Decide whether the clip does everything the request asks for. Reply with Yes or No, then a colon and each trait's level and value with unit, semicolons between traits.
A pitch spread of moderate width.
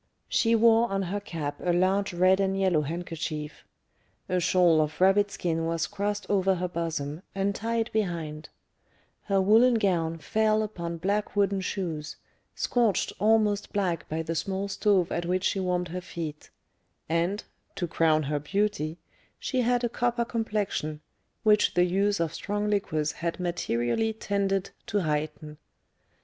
Yes: average, 3.8 semitones